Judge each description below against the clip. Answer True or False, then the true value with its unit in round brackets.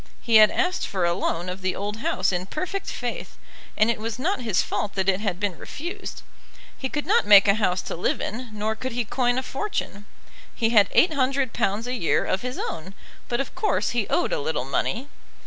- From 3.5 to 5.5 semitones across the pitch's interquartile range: True (5.2 semitones)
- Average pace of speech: False (215 wpm)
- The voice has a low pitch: False (220 Hz)